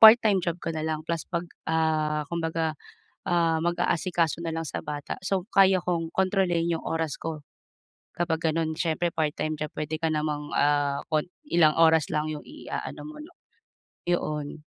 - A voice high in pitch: No, medium, 160 Hz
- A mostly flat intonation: Yes, narrow, 2.0 semitones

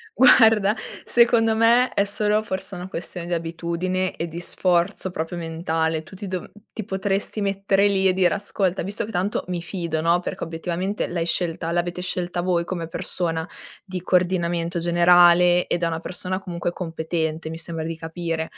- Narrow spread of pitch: Yes, narrow, 2.3 semitones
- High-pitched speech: No, medium, 175 Hz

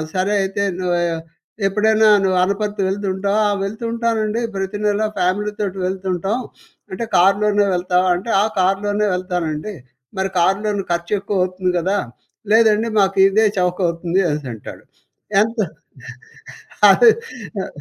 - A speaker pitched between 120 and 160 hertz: No, high, 195 Hz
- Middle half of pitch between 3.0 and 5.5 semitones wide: No, narrow, 2.4 semitones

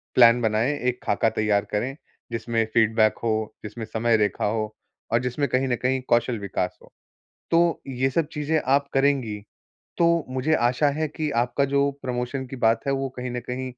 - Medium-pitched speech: No, low, 125 Hz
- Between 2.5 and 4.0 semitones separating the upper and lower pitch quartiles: Yes, average, 3.4 semitones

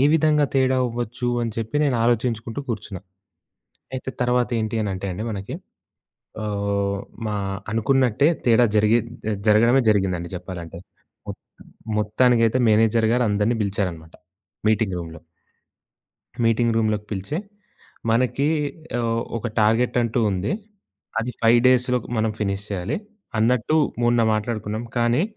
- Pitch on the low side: Yes, low, 115 Hz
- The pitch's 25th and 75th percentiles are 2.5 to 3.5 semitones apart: Yes, average, 2.8 semitones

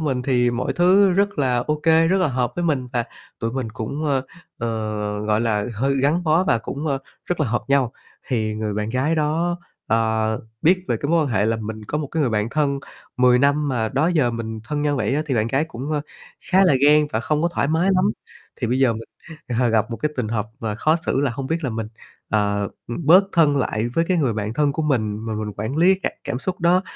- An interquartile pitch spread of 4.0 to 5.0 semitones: No, wide, 5.5 semitones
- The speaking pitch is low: Yes, low, 130 Hz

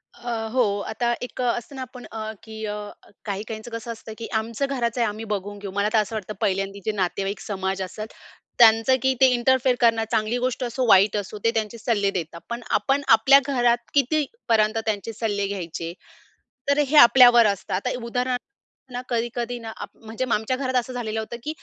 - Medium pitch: No, high, 225 Hz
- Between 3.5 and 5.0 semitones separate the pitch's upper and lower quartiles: No, average, 2.8 semitones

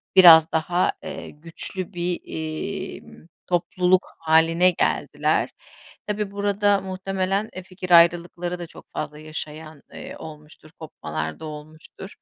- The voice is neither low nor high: Yes, medium, 175 Hz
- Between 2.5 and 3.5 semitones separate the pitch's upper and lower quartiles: Yes, average, 3.0 semitones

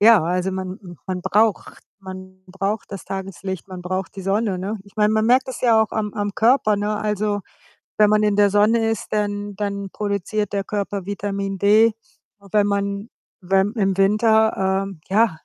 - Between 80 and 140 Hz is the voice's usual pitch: No, high, 200 Hz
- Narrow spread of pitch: Yes, narrow, 1.8 semitones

